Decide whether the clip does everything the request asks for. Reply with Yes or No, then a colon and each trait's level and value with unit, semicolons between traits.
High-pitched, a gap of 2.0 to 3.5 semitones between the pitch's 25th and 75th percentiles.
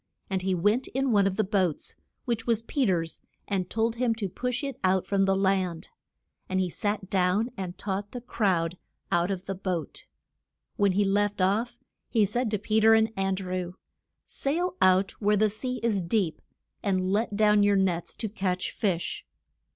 Yes: high, 200 Hz; average, 3.0 semitones